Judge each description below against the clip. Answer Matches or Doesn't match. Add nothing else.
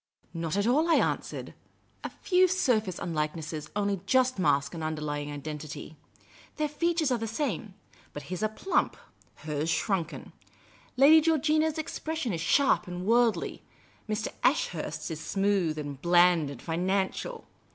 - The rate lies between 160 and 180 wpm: Doesn't match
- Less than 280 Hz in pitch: Matches